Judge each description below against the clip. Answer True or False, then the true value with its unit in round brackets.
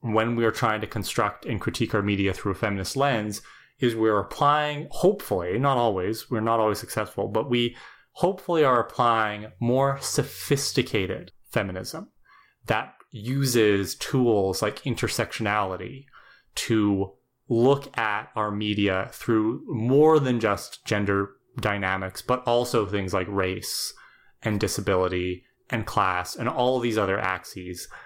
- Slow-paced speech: True (130 wpm)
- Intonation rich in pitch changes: False (3.6 semitones)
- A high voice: False (110 Hz)